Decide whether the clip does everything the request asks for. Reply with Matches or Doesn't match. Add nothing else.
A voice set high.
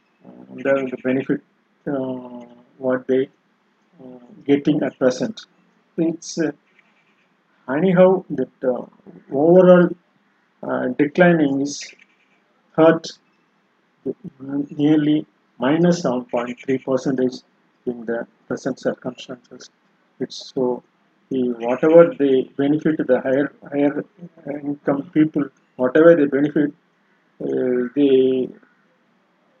Doesn't match